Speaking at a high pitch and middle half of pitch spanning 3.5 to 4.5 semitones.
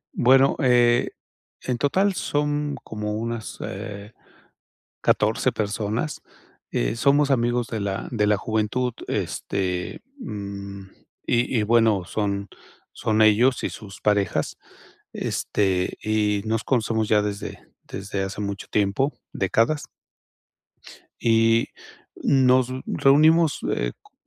No: low, 110 Hz; average, 3.8 semitones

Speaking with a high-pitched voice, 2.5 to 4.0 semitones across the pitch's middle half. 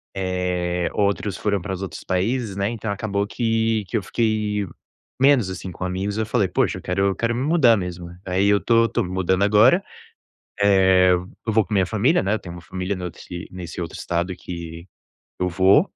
No: low, 100 Hz; average, 3.1 semitones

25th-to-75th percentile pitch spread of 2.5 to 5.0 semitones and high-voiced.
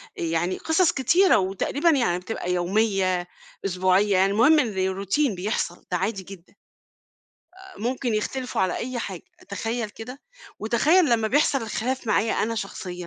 No: wide, 5.4 semitones; high, 215 Hz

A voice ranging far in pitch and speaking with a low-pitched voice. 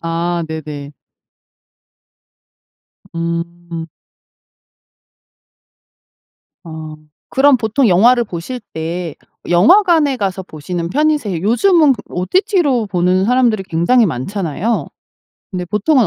No: wide, 7.0 semitones; high, 190 Hz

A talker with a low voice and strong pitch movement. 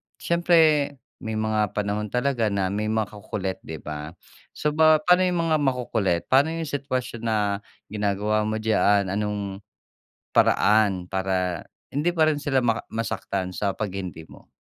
Yes: low, 110 Hz; wide, 6.0 semitones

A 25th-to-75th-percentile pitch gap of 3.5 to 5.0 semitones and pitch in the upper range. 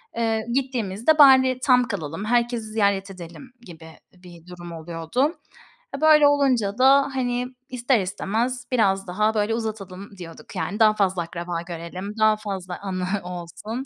No: wide, 5.4 semitones; high, 210 Hz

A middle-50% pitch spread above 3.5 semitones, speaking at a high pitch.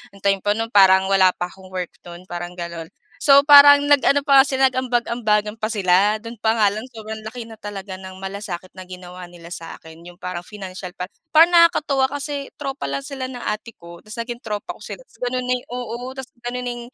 Yes: average, 5.1 semitones; high, 215 Hz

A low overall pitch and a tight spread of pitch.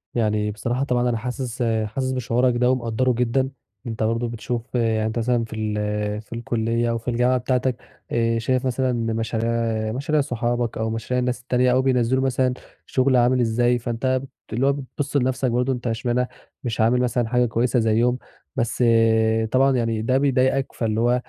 Yes: low, 120 Hz; narrow, 1.9 semitones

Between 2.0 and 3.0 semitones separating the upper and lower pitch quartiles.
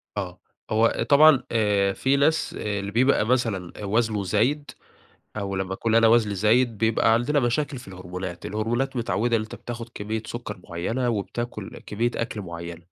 No: average, 3.4 semitones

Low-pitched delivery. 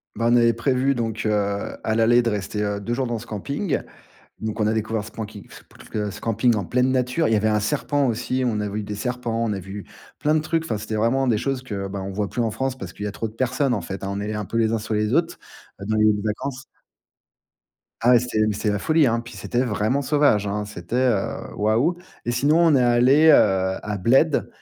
Yes: low, 115 Hz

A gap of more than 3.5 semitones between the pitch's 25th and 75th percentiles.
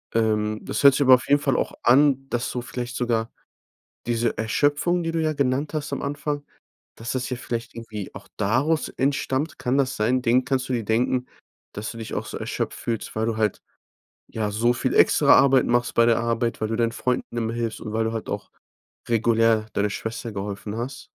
No: average, 2.9 semitones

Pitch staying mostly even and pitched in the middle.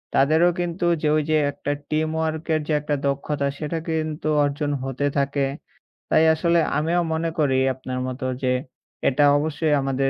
Yes: narrow, 2.3 semitones; medium, 150 Hz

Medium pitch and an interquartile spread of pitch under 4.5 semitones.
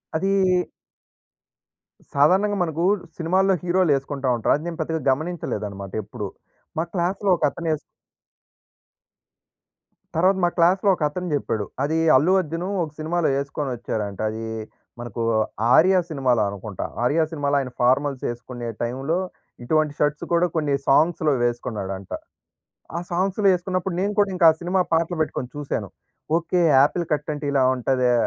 No: medium, 155 Hz; average, 5.3 semitones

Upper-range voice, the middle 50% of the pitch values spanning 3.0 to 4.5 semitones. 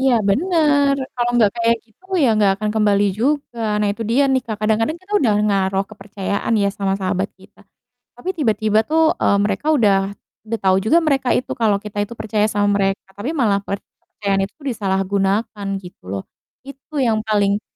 Yes: high, 215 Hz; average, 4.0 semitones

